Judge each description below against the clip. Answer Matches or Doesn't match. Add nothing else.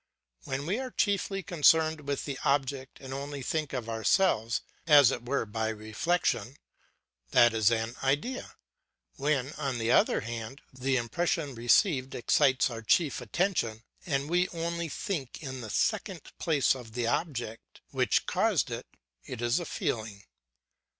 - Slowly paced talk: Doesn't match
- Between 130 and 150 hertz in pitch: Matches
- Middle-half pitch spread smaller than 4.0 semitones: Doesn't match